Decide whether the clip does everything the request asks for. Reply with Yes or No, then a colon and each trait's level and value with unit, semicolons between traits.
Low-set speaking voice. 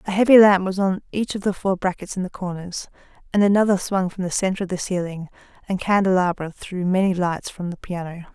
No: medium, 185 Hz